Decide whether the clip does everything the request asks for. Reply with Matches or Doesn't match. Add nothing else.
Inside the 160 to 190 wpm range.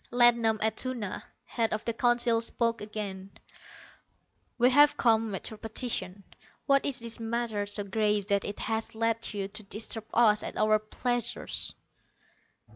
Doesn't match